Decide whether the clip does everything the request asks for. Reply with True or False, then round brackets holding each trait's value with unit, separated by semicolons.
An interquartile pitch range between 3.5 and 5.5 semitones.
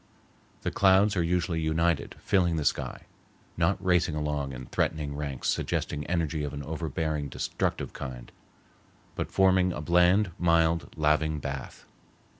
False (3.0 semitones)